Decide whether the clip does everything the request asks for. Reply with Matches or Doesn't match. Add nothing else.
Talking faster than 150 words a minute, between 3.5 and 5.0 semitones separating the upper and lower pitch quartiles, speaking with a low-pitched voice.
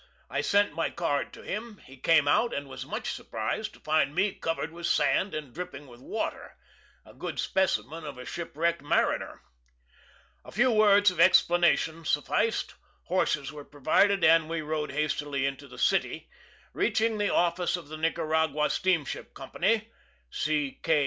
Doesn't match